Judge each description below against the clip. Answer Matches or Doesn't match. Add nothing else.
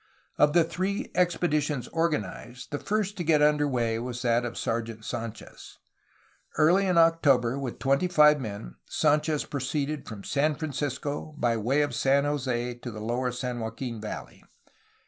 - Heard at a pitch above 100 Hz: Matches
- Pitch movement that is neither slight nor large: Matches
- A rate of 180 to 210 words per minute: Doesn't match